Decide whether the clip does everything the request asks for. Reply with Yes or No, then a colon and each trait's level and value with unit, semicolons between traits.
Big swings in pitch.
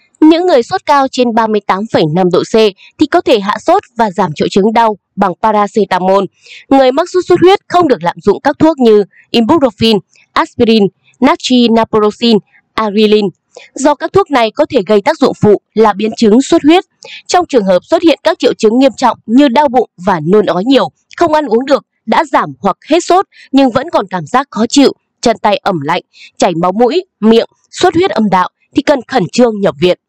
Yes: wide, 6.3 semitones